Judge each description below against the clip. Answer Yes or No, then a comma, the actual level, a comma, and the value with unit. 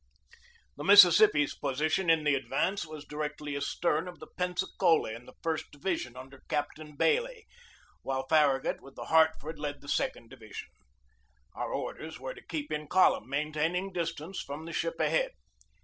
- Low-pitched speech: No, medium, 155 Hz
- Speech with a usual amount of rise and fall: Yes, average, 3.7 semitones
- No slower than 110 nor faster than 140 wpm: No, average, 160 wpm